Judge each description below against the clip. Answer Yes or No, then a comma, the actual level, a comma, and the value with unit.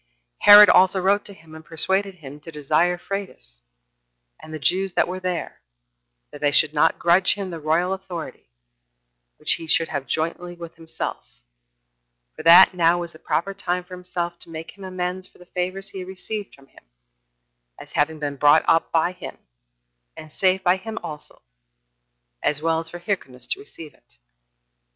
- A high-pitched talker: No, medium, 175 Hz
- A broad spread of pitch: No, average, 2.9 semitones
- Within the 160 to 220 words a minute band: Yes, average, 180 wpm